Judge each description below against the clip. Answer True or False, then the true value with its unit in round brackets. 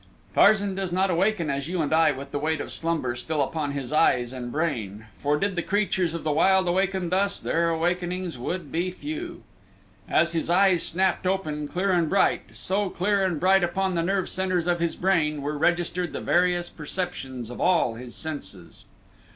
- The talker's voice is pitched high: False (170 Hz)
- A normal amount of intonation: True (3.9 semitones)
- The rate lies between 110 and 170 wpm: False (190 wpm)